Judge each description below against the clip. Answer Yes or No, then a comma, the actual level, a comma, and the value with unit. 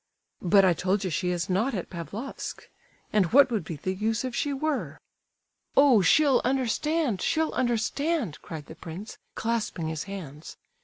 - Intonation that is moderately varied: No, wide, 6.8 semitones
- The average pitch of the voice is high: Yes, high, 210 Hz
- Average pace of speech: Yes, average, 160 wpm